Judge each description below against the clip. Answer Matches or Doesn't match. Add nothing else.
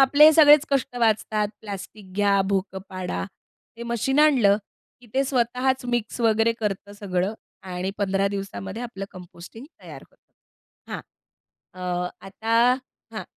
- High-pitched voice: Matches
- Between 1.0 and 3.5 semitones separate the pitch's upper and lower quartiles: Doesn't match